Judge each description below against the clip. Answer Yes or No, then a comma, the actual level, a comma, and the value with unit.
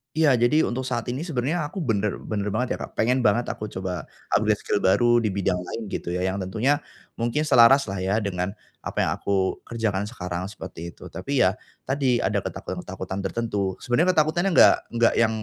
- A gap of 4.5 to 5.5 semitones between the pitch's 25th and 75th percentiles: Yes, average, 5.0 semitones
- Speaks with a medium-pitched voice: No, low, 115 Hz